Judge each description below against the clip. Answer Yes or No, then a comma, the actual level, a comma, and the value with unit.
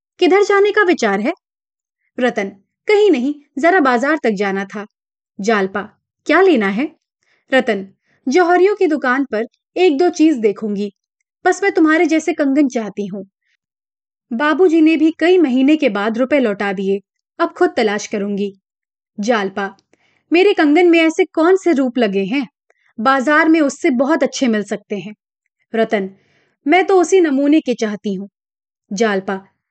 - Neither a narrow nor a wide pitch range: No, wide, 8.0 semitones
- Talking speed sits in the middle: Yes, average, 150 wpm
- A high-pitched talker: Yes, very high, 270 Hz